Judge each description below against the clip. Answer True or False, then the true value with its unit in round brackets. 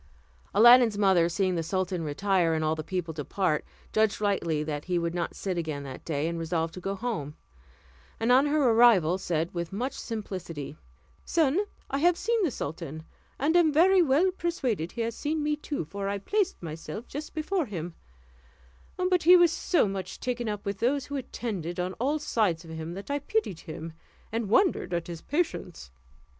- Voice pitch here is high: True (200 Hz)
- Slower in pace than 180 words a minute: False (185 wpm)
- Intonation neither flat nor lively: False (9.0 semitones)